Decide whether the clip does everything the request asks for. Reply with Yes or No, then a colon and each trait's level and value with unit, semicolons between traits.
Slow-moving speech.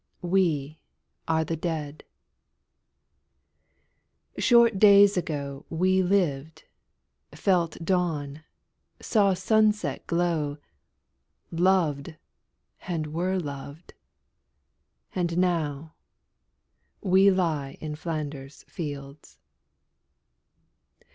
Yes: slow, 70 wpm